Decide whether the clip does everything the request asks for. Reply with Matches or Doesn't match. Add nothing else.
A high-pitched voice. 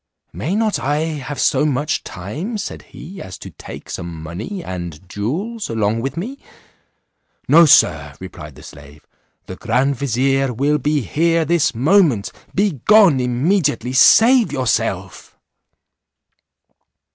Doesn't match